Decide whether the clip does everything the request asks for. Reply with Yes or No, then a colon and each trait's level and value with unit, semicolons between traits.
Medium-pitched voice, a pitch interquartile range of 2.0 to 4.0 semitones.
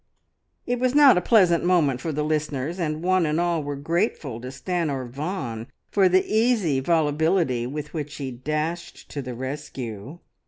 No: medium, 155 Hz; average, 4.5 semitones